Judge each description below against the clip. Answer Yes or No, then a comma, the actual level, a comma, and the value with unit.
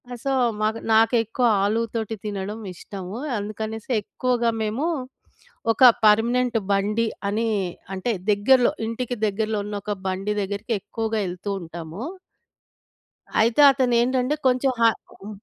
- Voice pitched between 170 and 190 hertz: No, high, 220 Hz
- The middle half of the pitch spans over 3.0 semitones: No, average, 2.7 semitones